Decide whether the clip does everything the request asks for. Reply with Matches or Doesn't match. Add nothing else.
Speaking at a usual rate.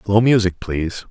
Matches